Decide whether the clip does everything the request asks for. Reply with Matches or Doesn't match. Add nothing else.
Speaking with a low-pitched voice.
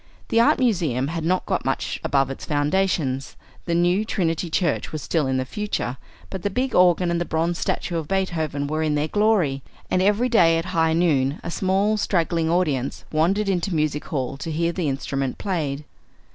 Doesn't match